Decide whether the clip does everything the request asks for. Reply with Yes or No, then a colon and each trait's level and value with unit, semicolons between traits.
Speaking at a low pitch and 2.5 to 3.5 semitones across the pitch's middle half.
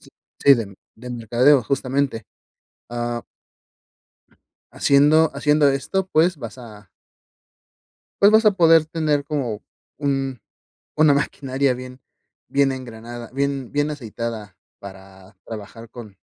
No: low, 130 Hz; average, 4.0 semitones